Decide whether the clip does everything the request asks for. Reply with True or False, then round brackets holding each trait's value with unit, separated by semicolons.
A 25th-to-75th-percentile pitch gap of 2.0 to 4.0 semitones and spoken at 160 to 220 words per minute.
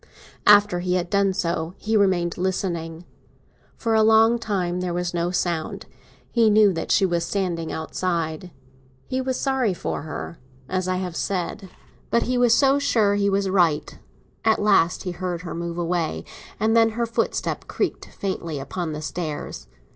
True (3.7 semitones; 170 wpm)